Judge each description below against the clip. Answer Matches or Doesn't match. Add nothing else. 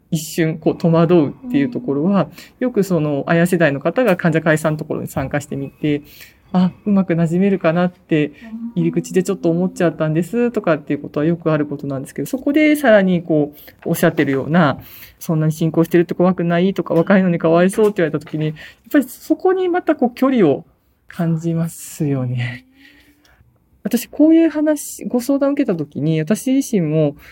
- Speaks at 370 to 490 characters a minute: Matches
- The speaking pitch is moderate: Matches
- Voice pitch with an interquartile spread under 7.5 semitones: Matches